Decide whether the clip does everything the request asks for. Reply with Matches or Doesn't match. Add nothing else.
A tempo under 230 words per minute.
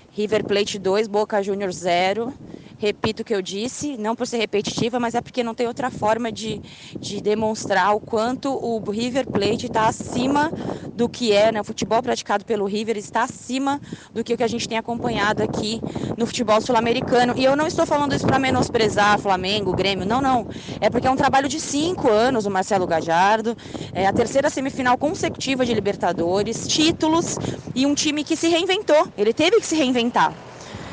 Matches